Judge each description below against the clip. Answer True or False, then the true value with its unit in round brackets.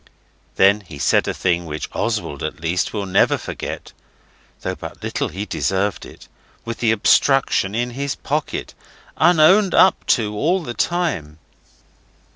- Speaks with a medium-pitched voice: False (105 Hz)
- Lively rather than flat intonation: True (7.9 semitones)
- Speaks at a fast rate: False (145 wpm)